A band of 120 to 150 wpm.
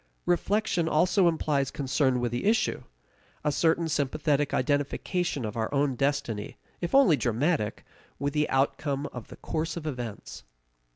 Yes: average, 140 wpm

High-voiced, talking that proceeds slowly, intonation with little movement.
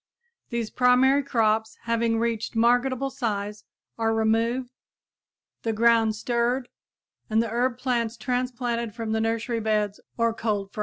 Yes: high, 230 Hz; slow, 130 wpm; narrow, 1.8 semitones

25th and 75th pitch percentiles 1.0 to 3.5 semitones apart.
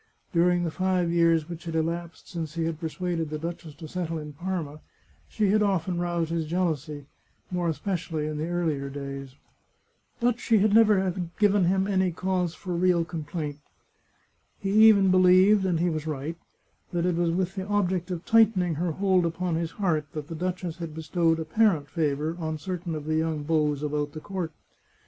Yes: average, 2.8 semitones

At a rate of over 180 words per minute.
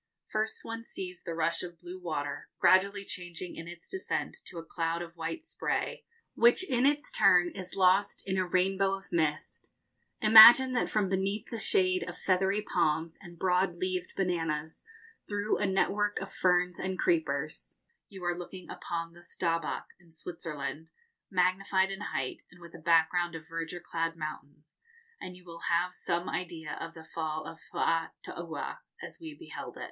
No: average, 170 wpm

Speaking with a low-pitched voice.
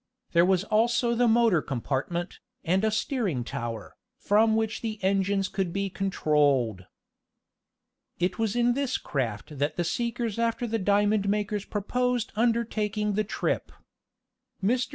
No: high, 205 Hz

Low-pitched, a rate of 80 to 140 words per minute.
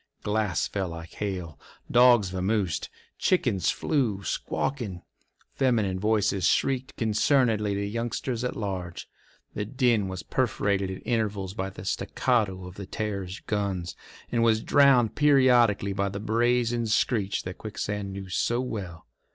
Yes: low, 105 Hz; slow, 135 wpm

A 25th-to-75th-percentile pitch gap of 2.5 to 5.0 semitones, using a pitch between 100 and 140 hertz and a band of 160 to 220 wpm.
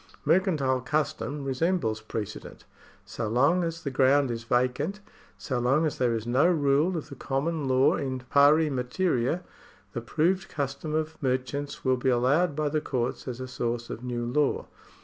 Yes: average, 3.7 semitones; low, 135 Hz; average, 175 wpm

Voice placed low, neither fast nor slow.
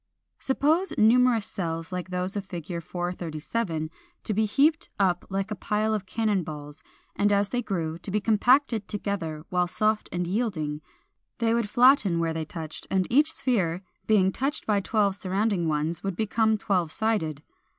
No: high, 195 Hz; average, 170 wpm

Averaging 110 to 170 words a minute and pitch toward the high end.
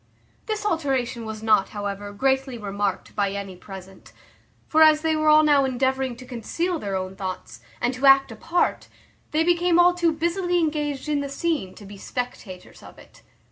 No: average, 180 wpm; very high, 265 Hz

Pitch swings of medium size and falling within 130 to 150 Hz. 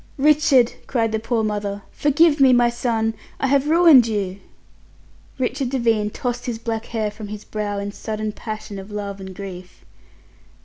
No: average, 3.4 semitones; high, 225 Hz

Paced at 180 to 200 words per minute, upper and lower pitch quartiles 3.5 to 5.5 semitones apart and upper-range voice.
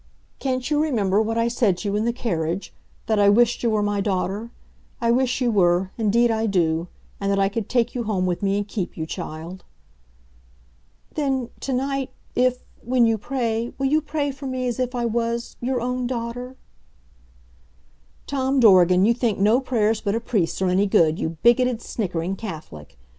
Yes: average, 190 wpm; average, 4.3 semitones; high, 225 Hz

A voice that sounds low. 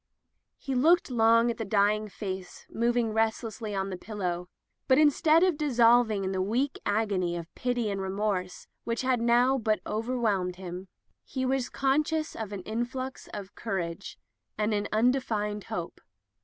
No: high, 220 Hz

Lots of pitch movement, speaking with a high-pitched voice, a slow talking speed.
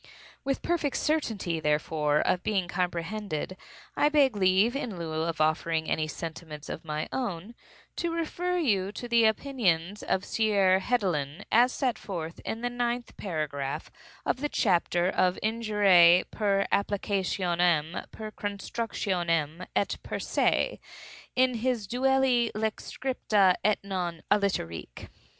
Yes: wide, 5.9 semitones; high, 195 Hz; slow, 130 wpm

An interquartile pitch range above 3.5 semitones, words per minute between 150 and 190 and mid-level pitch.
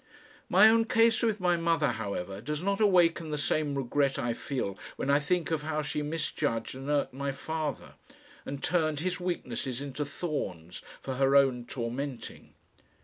Yes: average, 4.0 semitones; average, 165 wpm; medium, 145 Hz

